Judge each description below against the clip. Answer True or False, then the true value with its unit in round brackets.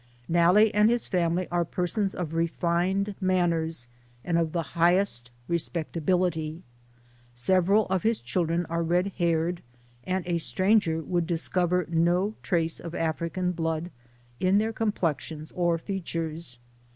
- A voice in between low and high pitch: True (175 Hz)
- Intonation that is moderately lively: False (2.1 semitones)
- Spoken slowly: True (125 wpm)